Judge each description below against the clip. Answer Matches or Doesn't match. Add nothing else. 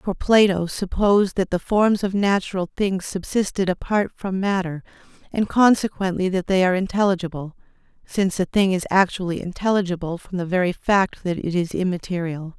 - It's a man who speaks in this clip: Doesn't match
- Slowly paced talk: Doesn't match